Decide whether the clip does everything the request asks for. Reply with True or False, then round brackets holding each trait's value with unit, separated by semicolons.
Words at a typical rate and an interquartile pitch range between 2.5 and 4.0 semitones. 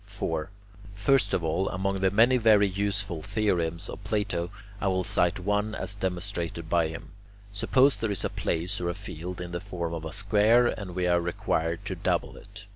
True (195 wpm; 3.0 semitones)